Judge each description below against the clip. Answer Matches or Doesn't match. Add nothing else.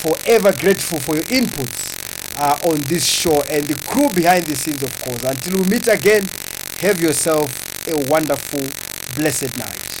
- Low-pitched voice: Doesn't match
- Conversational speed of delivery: Matches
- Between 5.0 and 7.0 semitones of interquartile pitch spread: Doesn't match